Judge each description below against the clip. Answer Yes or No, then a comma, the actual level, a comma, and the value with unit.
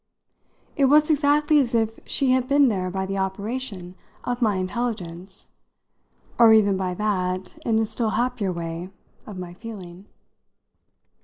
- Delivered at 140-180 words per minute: Yes, average, 145 wpm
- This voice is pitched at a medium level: No, high, 215 Hz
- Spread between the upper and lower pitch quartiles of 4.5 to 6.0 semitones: Yes, average, 4.9 semitones